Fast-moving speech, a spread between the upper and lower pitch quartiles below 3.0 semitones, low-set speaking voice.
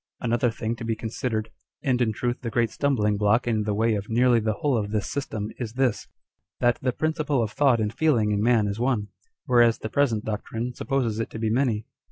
Yes: fast, 220 wpm; narrow, 2.5 semitones; low, 115 Hz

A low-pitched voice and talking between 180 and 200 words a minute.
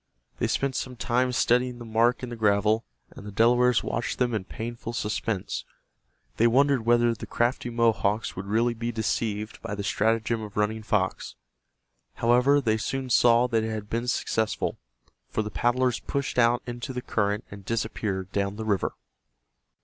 No: low, 115 Hz; average, 170 wpm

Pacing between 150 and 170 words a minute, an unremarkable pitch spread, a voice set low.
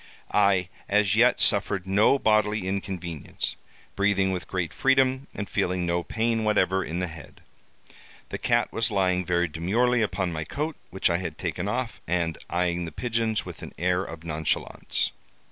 Yes: average, 160 wpm; average, 3.6 semitones; very low, 95 Hz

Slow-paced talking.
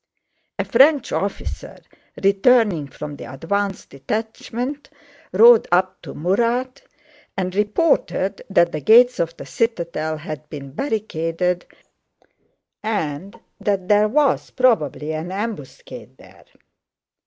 Yes: slow, 110 wpm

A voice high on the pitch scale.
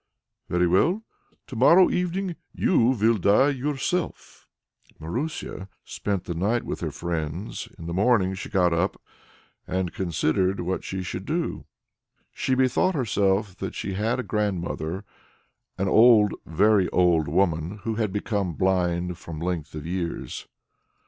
No: very low, 95 Hz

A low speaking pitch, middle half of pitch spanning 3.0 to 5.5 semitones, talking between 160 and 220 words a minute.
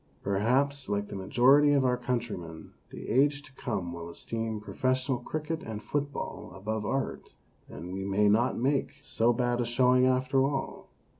Yes: low, 125 Hz; average, 4.4 semitones; average, 165 wpm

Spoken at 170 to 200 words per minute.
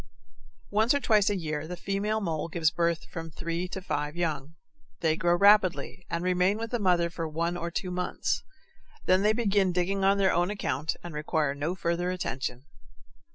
Yes: average, 190 wpm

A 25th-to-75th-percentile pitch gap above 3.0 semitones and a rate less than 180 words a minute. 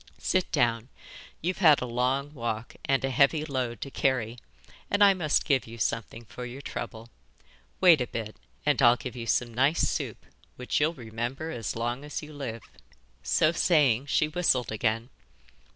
Yes: average, 4.2 semitones; average, 170 wpm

